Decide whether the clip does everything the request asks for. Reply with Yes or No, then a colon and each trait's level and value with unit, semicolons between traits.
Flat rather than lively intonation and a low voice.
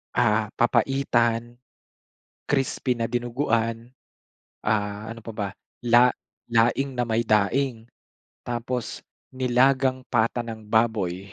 Yes: narrow, 2.0 semitones; low, 120 Hz